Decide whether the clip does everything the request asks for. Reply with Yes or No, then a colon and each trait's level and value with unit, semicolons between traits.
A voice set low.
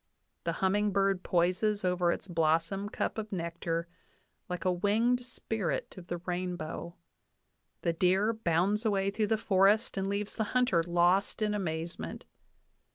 No: high, 190 Hz